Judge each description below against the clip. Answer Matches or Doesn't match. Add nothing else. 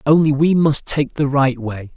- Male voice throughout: Matches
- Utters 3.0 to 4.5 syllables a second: Matches